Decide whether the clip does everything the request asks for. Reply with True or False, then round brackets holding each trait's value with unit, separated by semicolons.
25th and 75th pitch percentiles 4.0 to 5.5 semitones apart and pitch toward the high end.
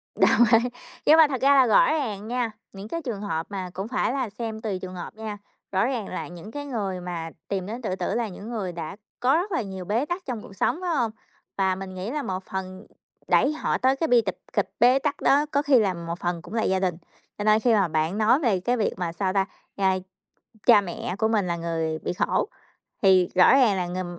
True (5.0 semitones; 205 Hz)